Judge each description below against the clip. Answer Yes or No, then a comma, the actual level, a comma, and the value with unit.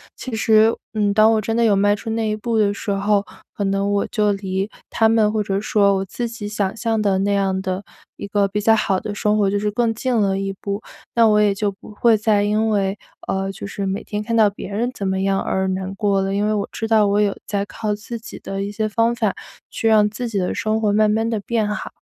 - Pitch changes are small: Yes, narrow, 1.7 semitones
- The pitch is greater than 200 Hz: Yes, high, 210 Hz